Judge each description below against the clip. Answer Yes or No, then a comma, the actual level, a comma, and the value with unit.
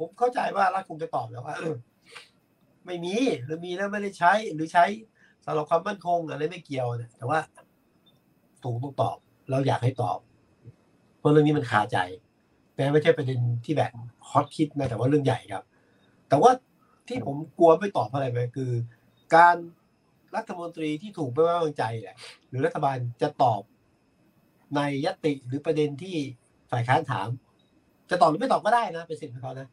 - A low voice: No, medium, 150 Hz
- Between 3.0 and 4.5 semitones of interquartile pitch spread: No, average, 5.0 semitones